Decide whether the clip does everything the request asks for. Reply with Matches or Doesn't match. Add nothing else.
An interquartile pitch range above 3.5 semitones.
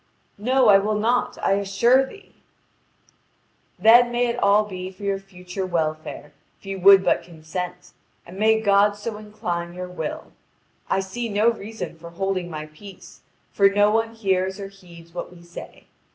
Doesn't match